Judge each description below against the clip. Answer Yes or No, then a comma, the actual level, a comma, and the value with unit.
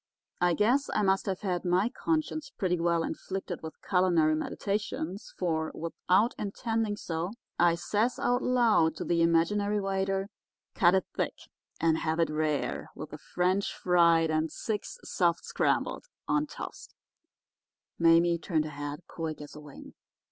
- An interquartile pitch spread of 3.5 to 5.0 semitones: Yes, average, 3.8 semitones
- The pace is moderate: Yes, average, 155 wpm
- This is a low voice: No, medium, 180 Hz